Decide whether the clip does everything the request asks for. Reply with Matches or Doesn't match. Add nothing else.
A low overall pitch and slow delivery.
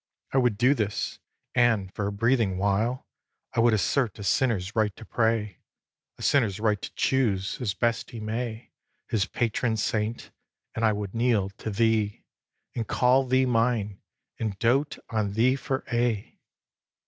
Doesn't match